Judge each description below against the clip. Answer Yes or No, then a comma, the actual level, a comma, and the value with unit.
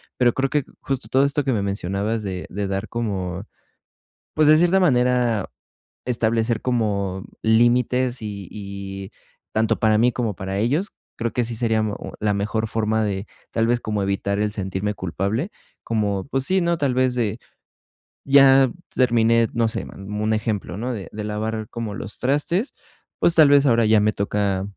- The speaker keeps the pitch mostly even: No, average, 3.6 semitones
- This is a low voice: Yes, low, 110 Hz